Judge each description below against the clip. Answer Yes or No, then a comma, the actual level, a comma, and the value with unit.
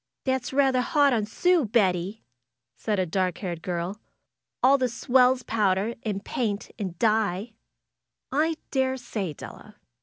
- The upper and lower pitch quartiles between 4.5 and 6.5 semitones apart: Yes, average, 5.2 semitones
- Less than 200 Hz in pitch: No, high, 220 Hz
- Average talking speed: No, slow, 125 wpm